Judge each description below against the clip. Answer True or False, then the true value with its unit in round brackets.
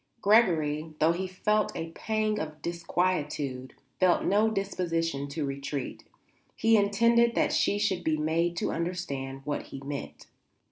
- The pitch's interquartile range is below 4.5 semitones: False (5.2 semitones)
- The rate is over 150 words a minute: False (140 wpm)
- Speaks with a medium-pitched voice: True (170 Hz)